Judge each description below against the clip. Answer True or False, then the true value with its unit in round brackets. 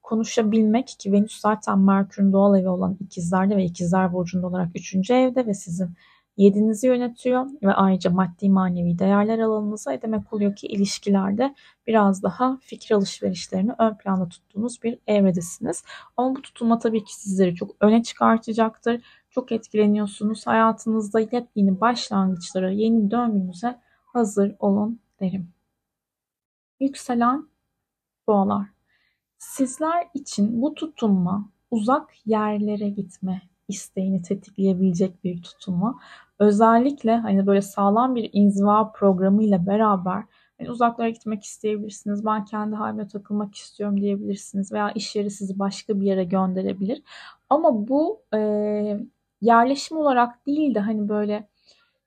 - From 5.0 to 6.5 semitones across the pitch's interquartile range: False (2.9 semitones)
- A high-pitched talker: True (210 Hz)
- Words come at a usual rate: True (120 wpm)